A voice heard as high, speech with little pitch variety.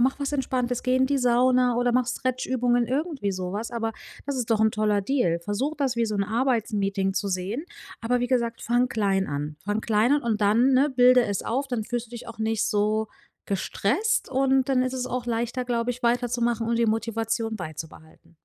No: high, 235 Hz; average, 3.0 semitones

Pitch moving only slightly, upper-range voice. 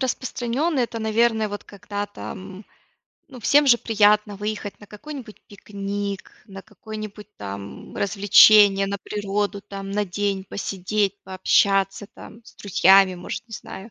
Yes: narrow, 1.8 semitones; high, 205 Hz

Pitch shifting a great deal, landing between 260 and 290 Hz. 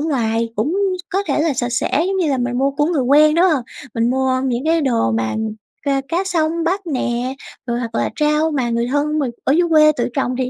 No: average, 4.4 semitones; very high, 275 Hz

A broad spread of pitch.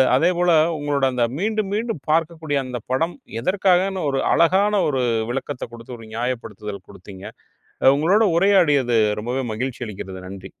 Yes: wide, 7.2 semitones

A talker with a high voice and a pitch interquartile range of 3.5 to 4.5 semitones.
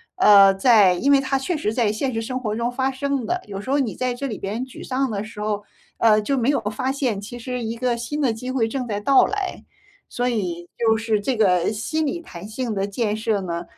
Yes: high, 230 Hz; average, 4.0 semitones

